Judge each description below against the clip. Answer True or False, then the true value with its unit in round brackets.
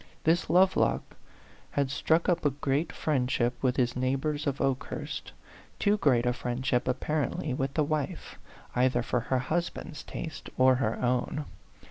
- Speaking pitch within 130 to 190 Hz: True (135 Hz)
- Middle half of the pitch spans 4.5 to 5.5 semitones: False (3.4 semitones)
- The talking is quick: False (145 wpm)